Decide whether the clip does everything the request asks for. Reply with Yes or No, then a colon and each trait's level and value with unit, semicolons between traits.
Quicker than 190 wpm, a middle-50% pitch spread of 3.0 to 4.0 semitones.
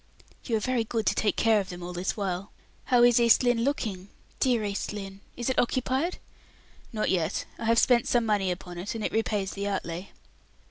Yes: fast, 205 wpm; average, 3.7 semitones